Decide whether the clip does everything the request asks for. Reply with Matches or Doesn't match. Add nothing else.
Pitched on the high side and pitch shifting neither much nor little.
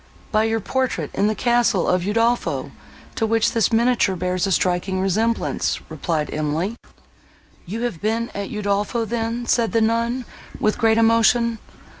Matches